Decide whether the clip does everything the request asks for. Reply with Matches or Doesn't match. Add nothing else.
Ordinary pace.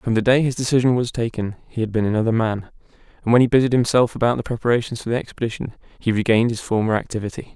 Doesn't match